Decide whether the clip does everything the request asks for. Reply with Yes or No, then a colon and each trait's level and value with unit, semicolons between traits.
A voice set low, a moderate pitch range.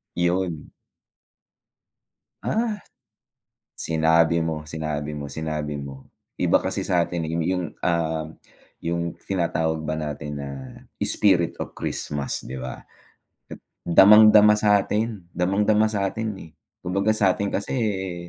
Yes: very low, 85 Hz; average, 4.2 semitones